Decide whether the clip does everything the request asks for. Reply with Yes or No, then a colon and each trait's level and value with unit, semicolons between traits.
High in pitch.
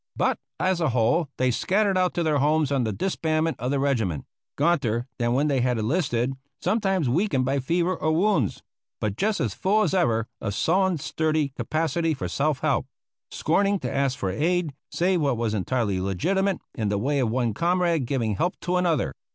No: medium, 145 Hz